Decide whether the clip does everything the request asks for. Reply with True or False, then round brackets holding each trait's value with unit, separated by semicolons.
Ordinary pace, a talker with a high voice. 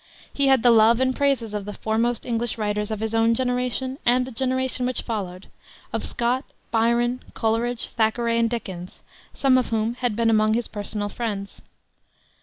True (175 wpm; 230 Hz)